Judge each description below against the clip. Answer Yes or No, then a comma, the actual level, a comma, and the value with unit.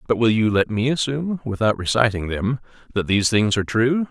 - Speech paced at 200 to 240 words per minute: Yes, fast, 205 wpm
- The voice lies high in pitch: No, low, 115 Hz